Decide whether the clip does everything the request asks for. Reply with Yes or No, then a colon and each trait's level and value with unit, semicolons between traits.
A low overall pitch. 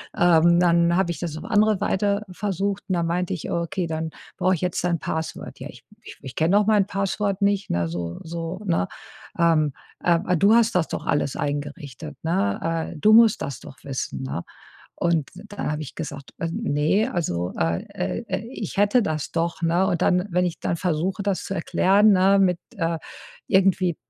No: medium, 170 Hz